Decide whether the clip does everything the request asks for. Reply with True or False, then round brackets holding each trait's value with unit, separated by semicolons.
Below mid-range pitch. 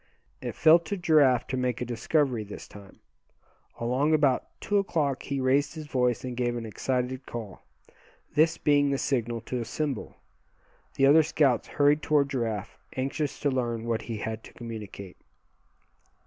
True (130 Hz)